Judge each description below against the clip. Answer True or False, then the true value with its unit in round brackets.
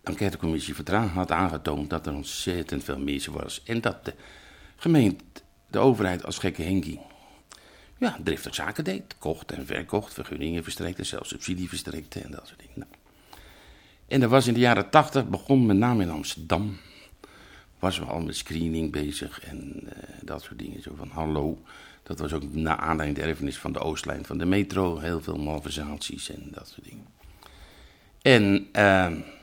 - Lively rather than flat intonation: False (4.2 semitones)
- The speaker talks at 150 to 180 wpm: True (170 wpm)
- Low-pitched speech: True (85 Hz)